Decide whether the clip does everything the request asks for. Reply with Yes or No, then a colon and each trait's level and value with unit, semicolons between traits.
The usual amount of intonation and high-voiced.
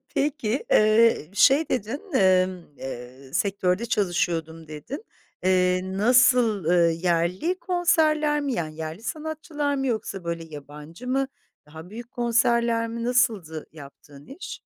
No: wide, 7.3 semitones; high, 210 Hz